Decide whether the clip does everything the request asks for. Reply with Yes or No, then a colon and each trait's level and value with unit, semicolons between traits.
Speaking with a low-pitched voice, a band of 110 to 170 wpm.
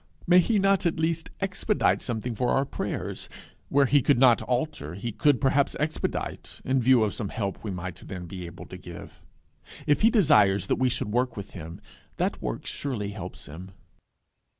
No: low, 125 Hz; average, 185 wpm